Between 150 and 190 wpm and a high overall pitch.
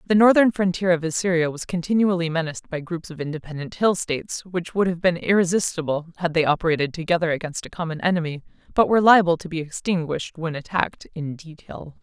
No: average, 185 wpm; medium, 170 Hz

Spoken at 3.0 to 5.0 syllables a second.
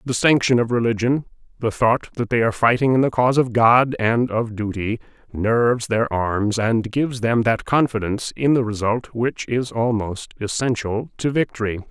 Yes: 4.9 syllables/s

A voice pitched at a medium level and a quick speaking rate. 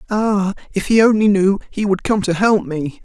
No: high, 200 Hz; fast, 215 wpm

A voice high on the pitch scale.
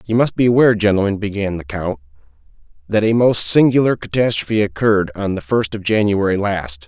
No: low, 100 Hz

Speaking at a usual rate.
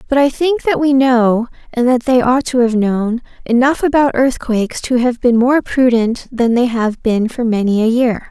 No: fast, 210 wpm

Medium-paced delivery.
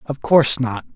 Yes: average, 190 wpm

